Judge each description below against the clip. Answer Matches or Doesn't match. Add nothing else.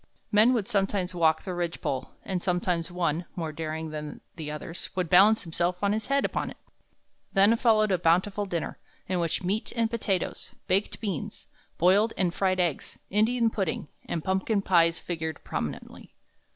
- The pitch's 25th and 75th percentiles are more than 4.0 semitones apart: Doesn't match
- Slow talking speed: Doesn't match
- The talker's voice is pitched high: Doesn't match